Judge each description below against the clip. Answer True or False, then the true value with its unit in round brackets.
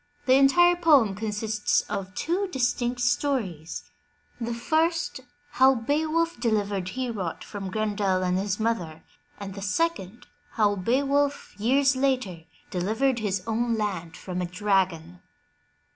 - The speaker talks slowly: True (130 wpm)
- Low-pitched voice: False (220 Hz)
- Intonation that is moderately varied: False (5.8 semitones)